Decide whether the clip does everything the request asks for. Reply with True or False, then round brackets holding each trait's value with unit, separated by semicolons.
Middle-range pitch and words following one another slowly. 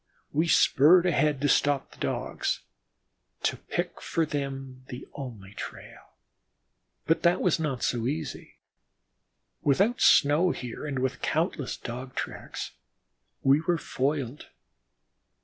True (145 Hz; 120 wpm)